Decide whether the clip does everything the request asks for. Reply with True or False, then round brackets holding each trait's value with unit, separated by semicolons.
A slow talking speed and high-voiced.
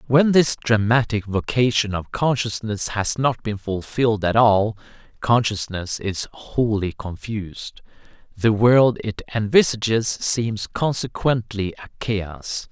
False (115 wpm; 110 Hz)